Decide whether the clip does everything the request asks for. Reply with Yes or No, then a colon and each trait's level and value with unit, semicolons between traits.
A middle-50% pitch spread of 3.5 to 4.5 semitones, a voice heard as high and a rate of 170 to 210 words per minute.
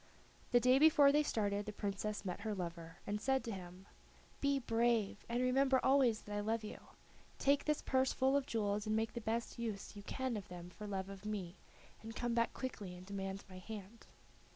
Yes: average, 4.2 semitones; high, 215 Hz; fast, 205 wpm